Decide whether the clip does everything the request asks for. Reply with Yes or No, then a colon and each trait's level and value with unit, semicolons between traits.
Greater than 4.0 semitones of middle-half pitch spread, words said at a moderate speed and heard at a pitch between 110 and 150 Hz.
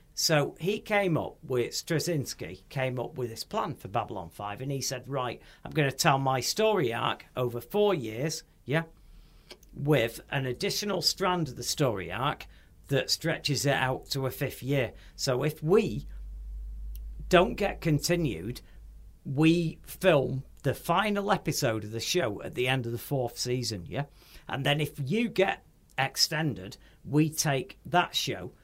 Yes: wide, 5.5 semitones; average, 160 wpm; medium, 140 Hz